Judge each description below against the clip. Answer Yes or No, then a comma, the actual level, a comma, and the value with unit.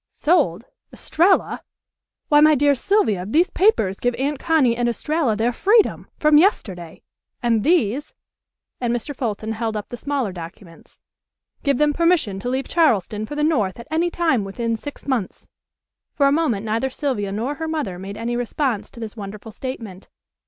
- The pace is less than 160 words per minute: No, average, 165 wpm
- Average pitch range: No, wide, 5.9 semitones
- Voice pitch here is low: No, high, 245 Hz